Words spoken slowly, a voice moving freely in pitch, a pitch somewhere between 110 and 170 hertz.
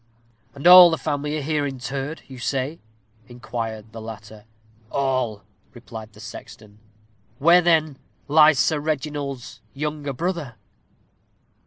No: slow, 120 wpm; average, 4.9 semitones; medium, 140 Hz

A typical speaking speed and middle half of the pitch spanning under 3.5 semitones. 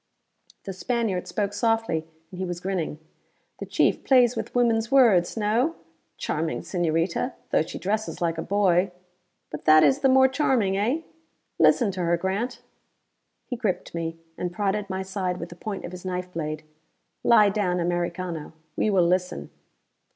No: average, 160 wpm; average, 4.2 semitones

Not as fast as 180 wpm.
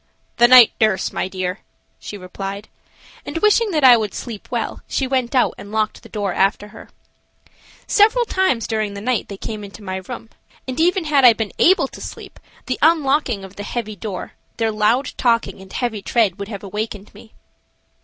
No: average, 190 wpm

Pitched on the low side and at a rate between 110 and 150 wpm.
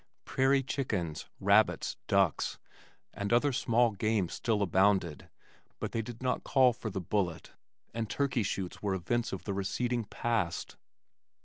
Yes: low, 110 Hz; average, 140 wpm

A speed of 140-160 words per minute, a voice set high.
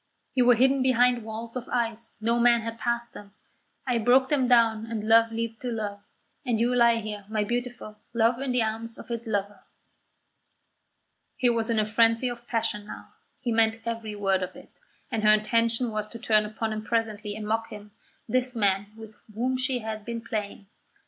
No: average, 195 wpm; high, 230 Hz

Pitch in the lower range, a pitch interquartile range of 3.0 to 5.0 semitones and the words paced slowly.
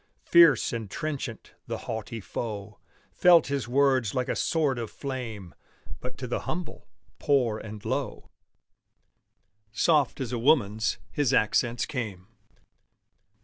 Yes: low, 125 Hz; average, 4.3 semitones; slow, 125 wpm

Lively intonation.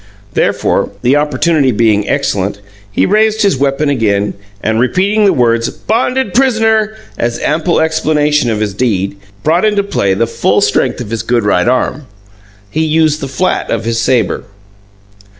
Yes: wide, 7.9 semitones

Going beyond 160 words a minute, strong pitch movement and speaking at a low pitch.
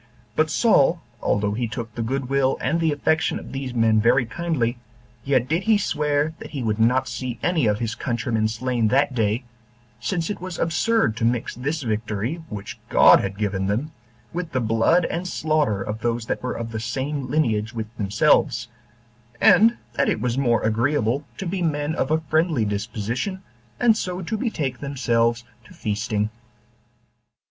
Yes: average, 175 wpm; wide, 5.8 semitones; low, 125 Hz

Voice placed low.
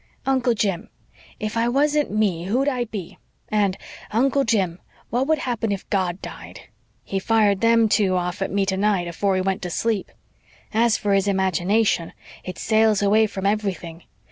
No: high, 205 Hz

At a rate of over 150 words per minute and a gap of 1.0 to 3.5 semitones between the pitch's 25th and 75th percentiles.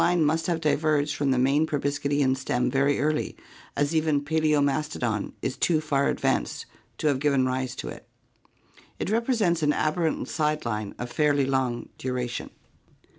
Yes: average, 160 wpm; average, 2.8 semitones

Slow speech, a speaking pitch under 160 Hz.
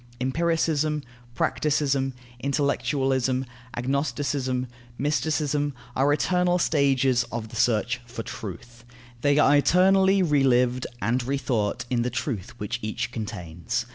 Yes: slow, 110 wpm; low, 135 Hz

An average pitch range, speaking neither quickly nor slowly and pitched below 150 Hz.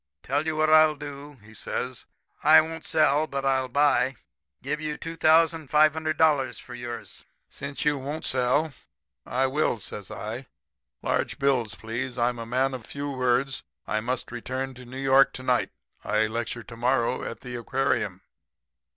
Yes: average, 3.3 semitones; average, 160 wpm; low, 135 Hz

